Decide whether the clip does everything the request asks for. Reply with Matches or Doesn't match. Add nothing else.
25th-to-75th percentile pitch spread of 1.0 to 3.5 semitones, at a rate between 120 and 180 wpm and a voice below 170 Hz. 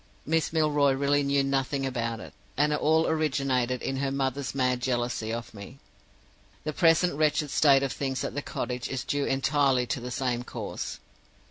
Matches